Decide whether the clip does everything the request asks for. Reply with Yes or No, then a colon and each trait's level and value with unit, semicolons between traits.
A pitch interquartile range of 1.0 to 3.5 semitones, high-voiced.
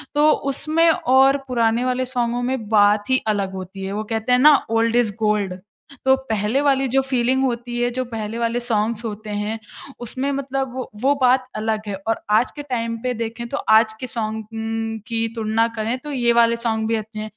Yes: average, 2.8 semitones; high, 235 Hz